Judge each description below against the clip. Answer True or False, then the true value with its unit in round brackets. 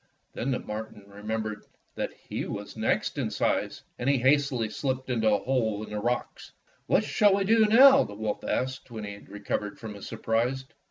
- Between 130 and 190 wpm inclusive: False (200 wpm)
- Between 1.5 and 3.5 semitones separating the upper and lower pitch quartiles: False (3.9 semitones)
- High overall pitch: False (115 Hz)